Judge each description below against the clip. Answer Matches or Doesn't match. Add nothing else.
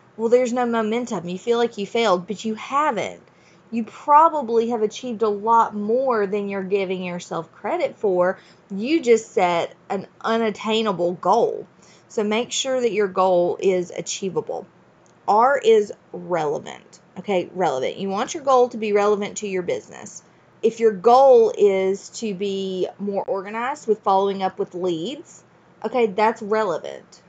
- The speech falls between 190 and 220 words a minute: Doesn't match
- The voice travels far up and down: Doesn't match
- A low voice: Doesn't match